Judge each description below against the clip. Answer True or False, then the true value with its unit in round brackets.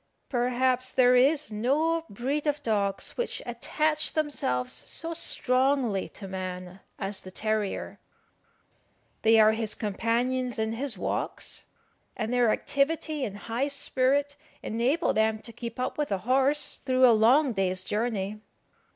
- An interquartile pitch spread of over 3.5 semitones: True (4.4 semitones)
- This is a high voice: True (245 Hz)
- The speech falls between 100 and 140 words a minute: True (135 wpm)